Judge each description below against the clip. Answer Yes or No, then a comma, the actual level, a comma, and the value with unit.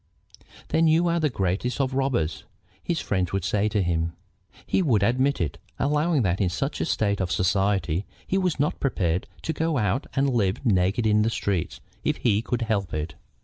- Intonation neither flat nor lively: No, wide, 6.7 semitones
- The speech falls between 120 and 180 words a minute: No, average, 190 wpm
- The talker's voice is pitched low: Yes, low, 105 Hz